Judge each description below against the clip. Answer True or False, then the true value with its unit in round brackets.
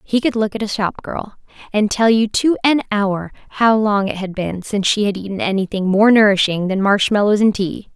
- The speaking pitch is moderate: False (205 Hz)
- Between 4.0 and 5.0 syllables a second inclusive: False (5.3 syllables/s)